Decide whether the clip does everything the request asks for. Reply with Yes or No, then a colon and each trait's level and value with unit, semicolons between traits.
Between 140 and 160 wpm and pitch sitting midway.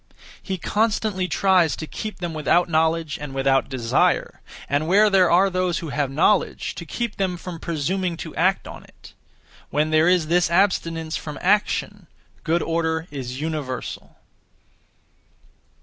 Yes: average, 150 wpm; medium, 165 Hz